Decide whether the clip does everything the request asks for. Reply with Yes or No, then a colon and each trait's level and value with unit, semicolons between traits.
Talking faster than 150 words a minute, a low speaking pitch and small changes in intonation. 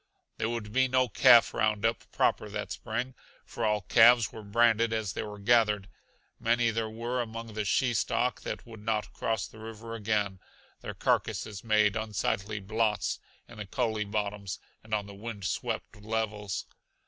Yes: average, 165 wpm; low, 110 Hz; narrow, 1.8 semitones